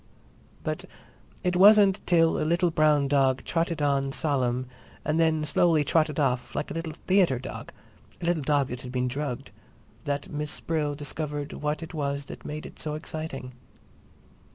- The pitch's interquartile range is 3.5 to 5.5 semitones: No, average, 2.7 semitones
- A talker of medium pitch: Yes, medium, 150 Hz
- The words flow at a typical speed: Yes, average, 165 wpm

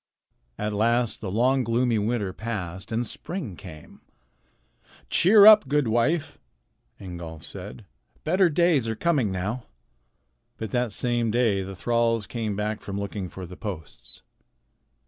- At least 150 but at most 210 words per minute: No, slow, 135 wpm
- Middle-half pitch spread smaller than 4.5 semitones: Yes, average, 4.1 semitones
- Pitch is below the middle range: Yes, low, 110 Hz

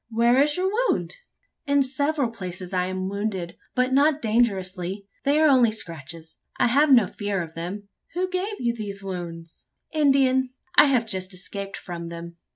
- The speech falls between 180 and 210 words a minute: No, average, 165 wpm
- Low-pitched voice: No, high, 215 Hz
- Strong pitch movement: Yes, wide, 6.9 semitones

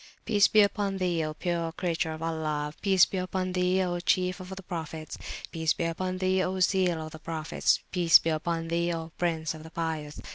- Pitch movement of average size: No, narrow, 2.3 semitones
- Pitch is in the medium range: Yes, medium, 170 Hz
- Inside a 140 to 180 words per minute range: No, fast, 205 wpm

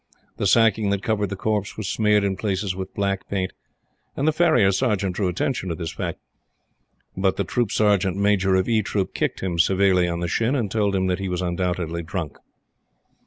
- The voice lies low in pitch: Yes, very low, 95 Hz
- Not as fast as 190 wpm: No, average, 200 wpm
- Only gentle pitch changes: Yes, narrow, 2.3 semitones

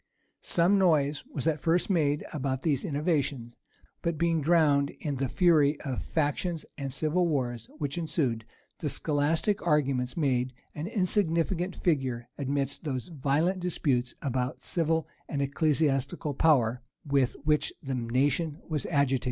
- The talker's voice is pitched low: No, medium, 145 Hz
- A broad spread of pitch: No, average, 3.4 semitones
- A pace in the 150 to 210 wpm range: No, slow, 135 wpm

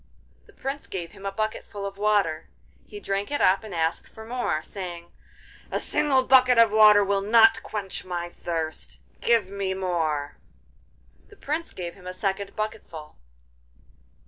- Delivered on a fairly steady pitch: No, average, 3.9 semitones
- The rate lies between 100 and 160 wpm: Yes, average, 155 wpm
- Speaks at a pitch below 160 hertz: No, high, 200 Hz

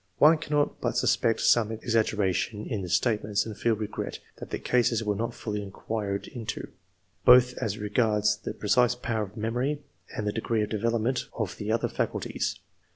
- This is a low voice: Yes, low, 110 Hz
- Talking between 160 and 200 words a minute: Yes, average, 175 wpm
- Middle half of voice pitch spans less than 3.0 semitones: Yes, narrow, 2.4 semitones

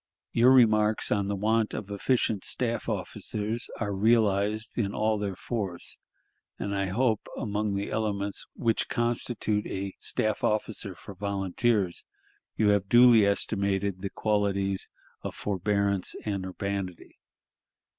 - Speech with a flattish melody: Yes, narrow, 1.9 semitones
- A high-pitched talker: No, low, 105 Hz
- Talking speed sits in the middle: No, slow, 125 wpm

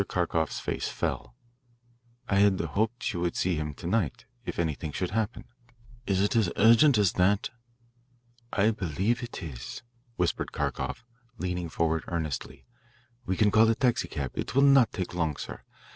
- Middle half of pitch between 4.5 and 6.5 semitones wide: Yes, average, 5.0 semitones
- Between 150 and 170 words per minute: Yes, average, 160 wpm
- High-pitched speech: No, very low, 95 Hz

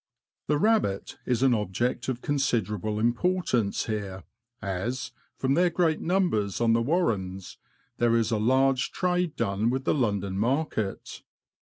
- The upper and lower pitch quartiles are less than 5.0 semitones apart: No, wide, 5.6 semitones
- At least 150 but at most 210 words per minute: No, average, 140 wpm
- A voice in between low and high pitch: No, low, 120 Hz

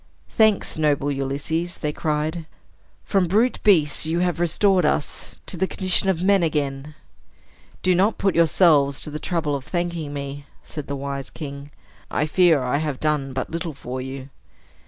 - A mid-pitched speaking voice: Yes, medium, 155 Hz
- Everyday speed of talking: Yes, average, 165 wpm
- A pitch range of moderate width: Yes, average, 3.8 semitones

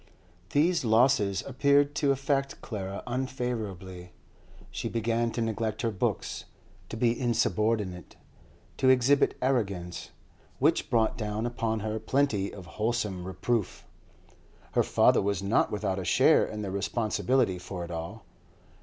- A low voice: Yes, low, 110 Hz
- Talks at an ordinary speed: No, slow, 130 wpm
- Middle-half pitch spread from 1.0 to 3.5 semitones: No, average, 4.0 semitones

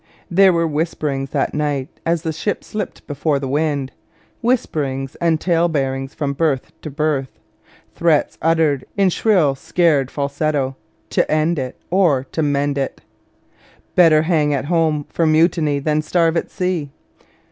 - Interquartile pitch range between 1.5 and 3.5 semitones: Yes, average, 3.0 semitones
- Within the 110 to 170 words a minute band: Yes, average, 145 wpm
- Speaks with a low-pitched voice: No, medium, 155 Hz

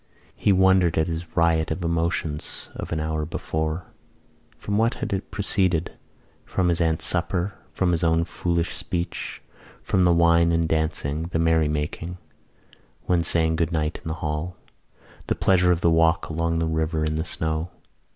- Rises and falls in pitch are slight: Yes, narrow, 1.7 semitones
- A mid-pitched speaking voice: No, very low, 85 Hz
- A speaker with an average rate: Yes, average, 170 wpm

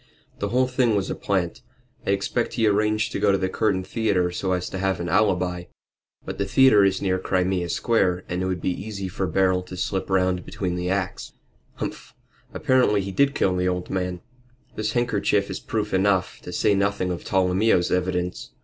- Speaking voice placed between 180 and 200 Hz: No, very low, 95 Hz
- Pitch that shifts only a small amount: Yes, narrow, 2.2 semitones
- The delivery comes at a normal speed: Yes, average, 195 wpm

